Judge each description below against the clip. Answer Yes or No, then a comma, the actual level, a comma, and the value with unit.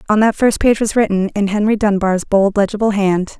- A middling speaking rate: No, fast, 210 wpm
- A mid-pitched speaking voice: No, high, 205 Hz